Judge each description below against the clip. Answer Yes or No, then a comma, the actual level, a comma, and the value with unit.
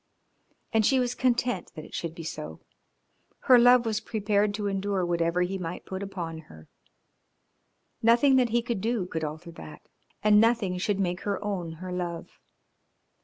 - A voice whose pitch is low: No, high, 195 Hz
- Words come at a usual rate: Yes, average, 170 wpm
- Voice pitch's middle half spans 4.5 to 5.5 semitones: Yes, average, 4.9 semitones